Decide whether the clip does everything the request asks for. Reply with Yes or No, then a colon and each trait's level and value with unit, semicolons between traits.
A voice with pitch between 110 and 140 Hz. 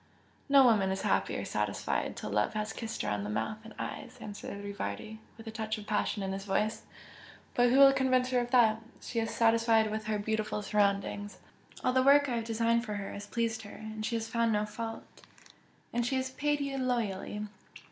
No: high, 225 Hz